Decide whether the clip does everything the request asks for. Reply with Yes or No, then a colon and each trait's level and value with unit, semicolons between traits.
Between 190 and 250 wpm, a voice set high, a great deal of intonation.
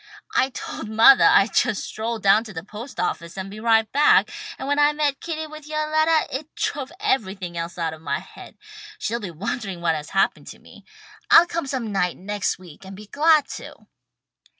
Yes: average, 200 wpm; high, 220 Hz; wide, 7.4 semitones